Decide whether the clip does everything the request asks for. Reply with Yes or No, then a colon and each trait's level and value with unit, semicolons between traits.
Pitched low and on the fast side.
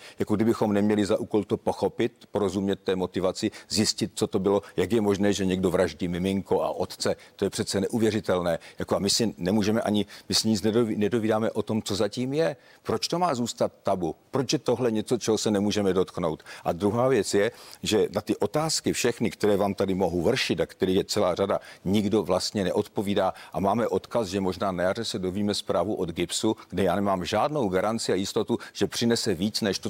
Yes: low, 105 Hz; fast, 205 wpm